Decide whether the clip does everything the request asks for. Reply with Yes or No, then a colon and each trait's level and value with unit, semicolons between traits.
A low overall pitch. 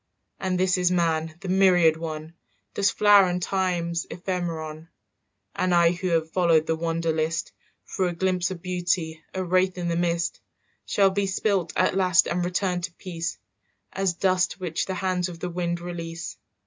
No: medium, 175 Hz